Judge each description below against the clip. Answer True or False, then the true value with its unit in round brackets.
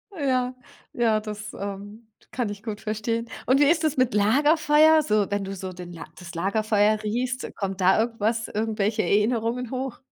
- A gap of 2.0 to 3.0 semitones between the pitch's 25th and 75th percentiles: False (3.5 semitones)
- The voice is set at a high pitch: True (220 Hz)